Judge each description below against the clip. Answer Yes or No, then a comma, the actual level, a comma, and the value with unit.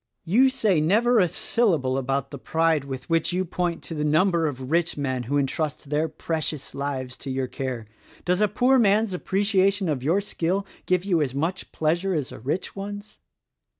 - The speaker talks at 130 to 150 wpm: No, average, 185 wpm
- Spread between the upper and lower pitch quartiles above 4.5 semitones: Yes, wide, 5.6 semitones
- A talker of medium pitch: Yes, medium, 165 Hz